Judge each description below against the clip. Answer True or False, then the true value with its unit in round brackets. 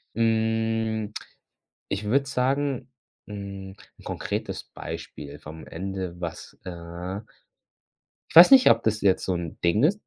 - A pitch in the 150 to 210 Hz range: False (105 Hz)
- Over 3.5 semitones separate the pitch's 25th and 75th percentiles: True (4.1 semitones)